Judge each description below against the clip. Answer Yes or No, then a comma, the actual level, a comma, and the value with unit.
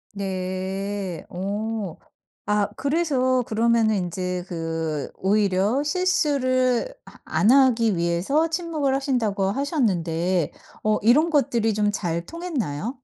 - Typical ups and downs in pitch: No, wide, 6.3 semitones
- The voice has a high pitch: Yes, high, 215 Hz